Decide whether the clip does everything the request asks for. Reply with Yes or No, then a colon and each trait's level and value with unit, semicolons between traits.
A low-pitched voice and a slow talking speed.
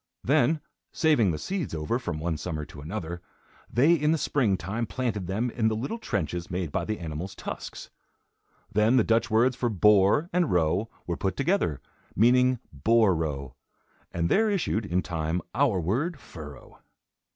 No: low, 105 Hz; average, 165 wpm